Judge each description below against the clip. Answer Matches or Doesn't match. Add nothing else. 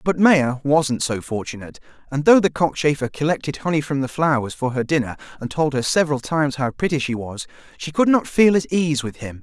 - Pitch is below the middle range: Doesn't match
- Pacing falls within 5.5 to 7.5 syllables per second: Matches